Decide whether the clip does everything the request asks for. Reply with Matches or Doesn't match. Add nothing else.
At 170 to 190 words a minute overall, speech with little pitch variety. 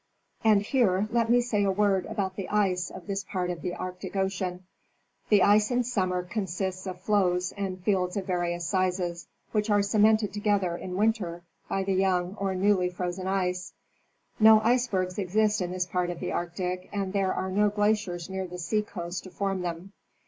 Matches